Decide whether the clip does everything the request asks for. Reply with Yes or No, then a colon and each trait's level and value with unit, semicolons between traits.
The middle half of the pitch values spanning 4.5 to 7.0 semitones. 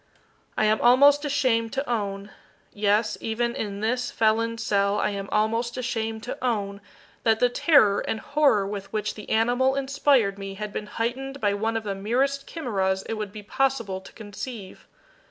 No: average, 3.5 semitones